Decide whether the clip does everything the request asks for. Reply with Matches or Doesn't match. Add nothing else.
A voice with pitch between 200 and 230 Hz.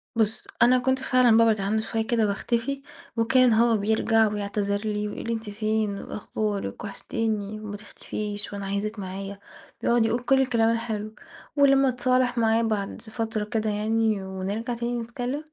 Matches